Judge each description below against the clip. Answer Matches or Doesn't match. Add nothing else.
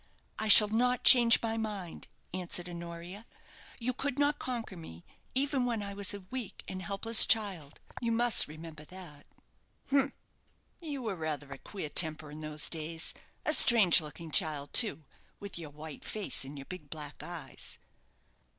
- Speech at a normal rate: Matches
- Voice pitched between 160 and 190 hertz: Matches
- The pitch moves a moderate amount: Doesn't match